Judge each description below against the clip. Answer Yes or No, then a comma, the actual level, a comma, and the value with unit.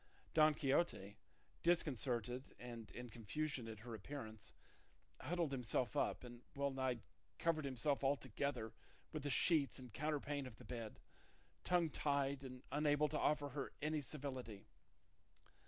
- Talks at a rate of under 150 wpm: Yes, slow, 135 wpm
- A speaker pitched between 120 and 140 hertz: Yes, low, 135 Hz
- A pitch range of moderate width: Yes, average, 3.4 semitones